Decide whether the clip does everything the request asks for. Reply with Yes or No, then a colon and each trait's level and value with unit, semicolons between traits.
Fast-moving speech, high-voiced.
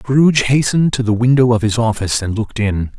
No: fast, 220 wpm; low, 120 Hz